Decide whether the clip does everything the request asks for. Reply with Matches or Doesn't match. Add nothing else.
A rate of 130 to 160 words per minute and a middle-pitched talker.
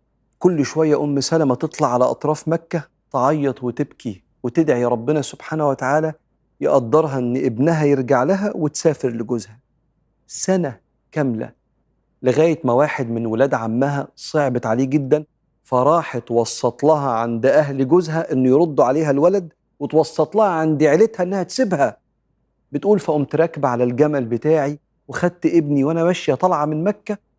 Matches